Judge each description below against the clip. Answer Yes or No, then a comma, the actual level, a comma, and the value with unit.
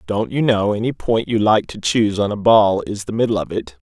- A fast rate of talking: Yes, fast, 265 wpm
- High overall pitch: No, low, 105 Hz